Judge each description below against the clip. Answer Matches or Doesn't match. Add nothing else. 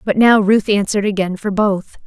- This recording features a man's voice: Doesn't match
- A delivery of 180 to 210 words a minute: Matches